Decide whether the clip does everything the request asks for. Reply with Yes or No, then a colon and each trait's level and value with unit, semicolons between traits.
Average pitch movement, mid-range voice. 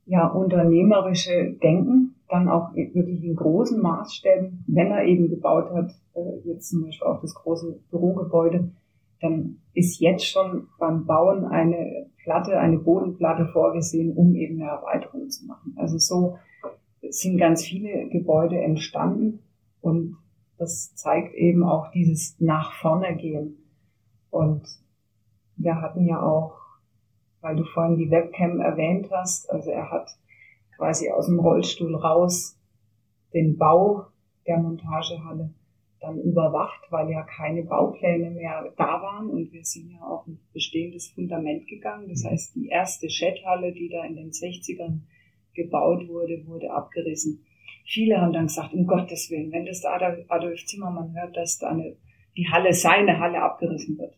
No: narrow, 1.8 semitones; medium, 170 Hz